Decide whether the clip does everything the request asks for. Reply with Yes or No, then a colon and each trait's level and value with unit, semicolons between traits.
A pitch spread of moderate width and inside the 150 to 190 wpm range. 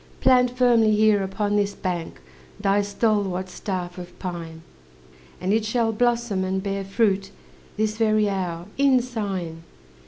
No: average, 3.0 semitones; slow, 135 wpm